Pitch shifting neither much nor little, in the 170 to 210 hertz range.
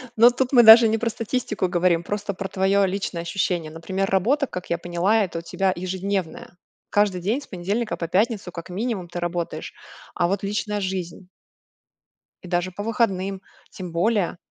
Yes: average, 3.1 semitones; high, 190 Hz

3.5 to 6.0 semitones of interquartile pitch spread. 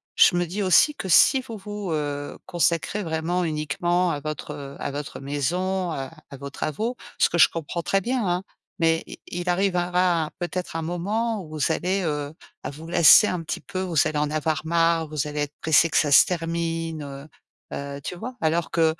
No: average, 3.1 semitones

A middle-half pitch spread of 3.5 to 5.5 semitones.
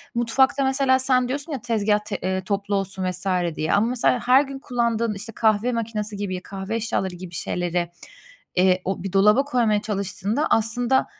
Yes: average, 4.2 semitones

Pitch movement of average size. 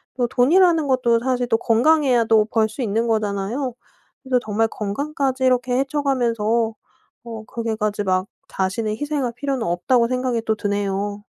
Yes: average, 3.4 semitones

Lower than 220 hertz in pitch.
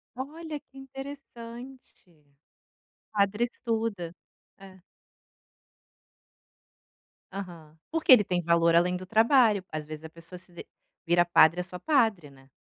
Yes: high, 190 Hz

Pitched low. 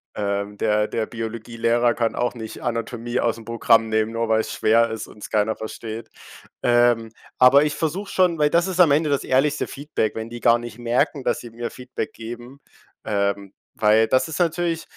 Yes: low, 115 Hz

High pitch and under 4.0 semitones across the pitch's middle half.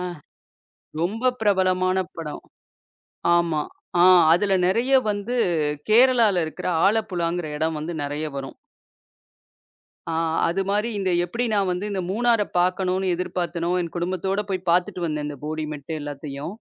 No: medium, 180 Hz; average, 3.5 semitones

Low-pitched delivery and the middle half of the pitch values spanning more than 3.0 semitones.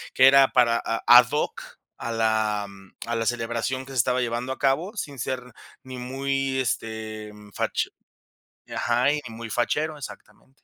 No: low, 125 Hz; average, 2.7 semitones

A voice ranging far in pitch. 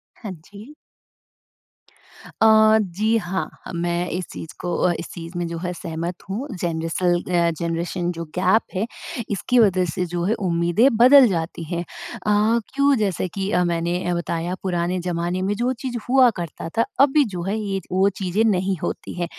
No: average, 3.8 semitones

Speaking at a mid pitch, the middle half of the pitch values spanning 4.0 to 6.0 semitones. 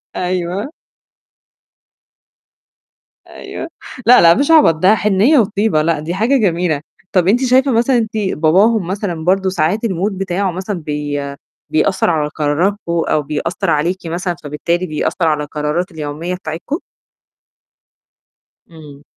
Yes: medium, 180 Hz; average, 4.6 semitones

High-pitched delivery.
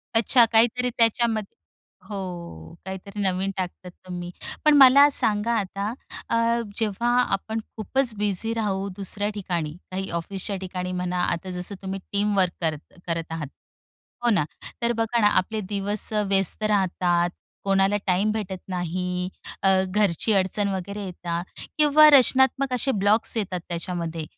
Yes: high, 195 Hz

